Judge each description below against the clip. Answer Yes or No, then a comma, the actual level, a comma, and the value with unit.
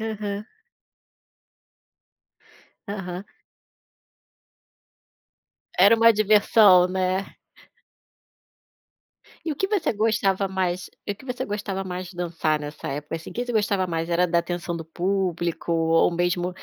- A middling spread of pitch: Yes, average, 3.1 semitones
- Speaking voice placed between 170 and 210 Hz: Yes, medium, 185 Hz